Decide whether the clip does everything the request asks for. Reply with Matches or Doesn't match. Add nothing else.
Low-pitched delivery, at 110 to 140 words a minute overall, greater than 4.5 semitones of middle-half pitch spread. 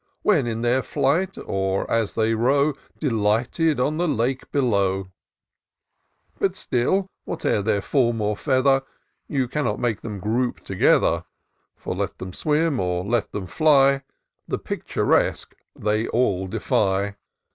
Matches